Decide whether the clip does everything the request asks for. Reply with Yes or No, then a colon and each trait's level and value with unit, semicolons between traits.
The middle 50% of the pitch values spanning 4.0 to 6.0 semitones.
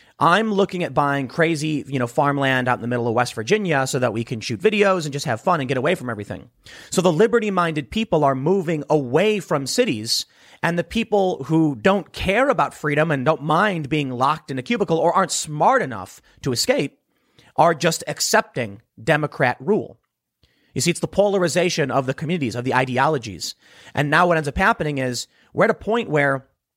Yes: average, 5.2 semitones